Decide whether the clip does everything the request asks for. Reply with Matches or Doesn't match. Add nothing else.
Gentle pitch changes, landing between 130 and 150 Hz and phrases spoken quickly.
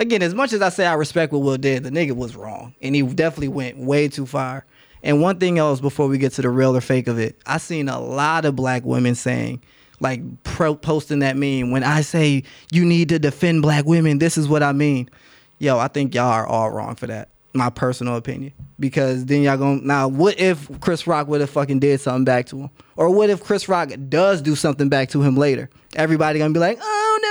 Doesn't match